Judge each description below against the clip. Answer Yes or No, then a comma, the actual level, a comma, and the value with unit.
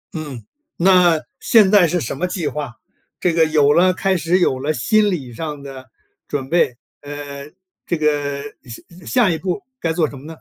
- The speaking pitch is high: No, medium, 155 Hz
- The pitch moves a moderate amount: Yes, average, 4.0 semitones